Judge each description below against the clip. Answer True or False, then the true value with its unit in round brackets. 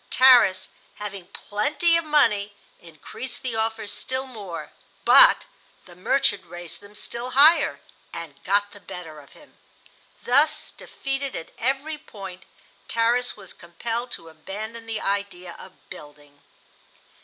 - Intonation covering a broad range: True (6.2 semitones)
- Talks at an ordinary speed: False (130 wpm)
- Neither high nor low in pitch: False (210 Hz)